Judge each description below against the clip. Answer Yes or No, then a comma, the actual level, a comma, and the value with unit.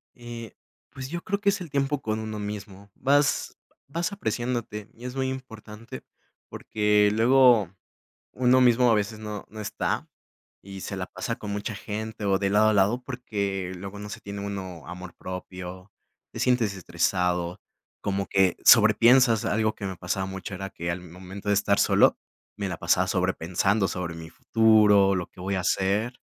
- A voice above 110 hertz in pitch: No, low, 105 Hz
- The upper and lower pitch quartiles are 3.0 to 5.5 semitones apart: Yes, average, 3.4 semitones